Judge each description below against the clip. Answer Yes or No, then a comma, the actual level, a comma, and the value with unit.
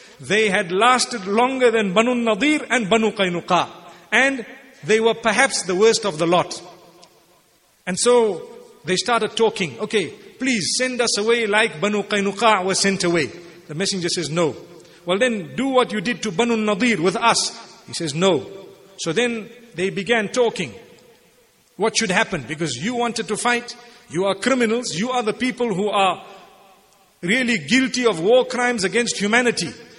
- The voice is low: No, high, 220 Hz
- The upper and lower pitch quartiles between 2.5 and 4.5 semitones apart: Yes, average, 3.9 semitones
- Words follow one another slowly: No, average, 165 wpm